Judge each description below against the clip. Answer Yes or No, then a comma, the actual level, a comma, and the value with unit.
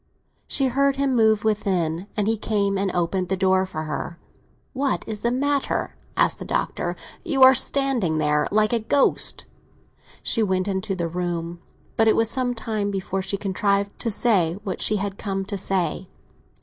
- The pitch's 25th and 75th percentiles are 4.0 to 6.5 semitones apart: No, average, 3.5 semitones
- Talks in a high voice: Yes, high, 200 Hz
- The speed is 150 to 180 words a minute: Yes, average, 175 wpm